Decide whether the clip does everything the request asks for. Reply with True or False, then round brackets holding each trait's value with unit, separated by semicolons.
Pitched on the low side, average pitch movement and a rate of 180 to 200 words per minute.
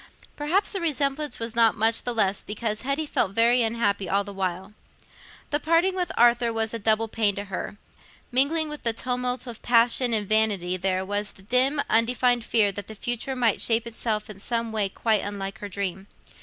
False (225 Hz; 3.5 semitones; 190 wpm)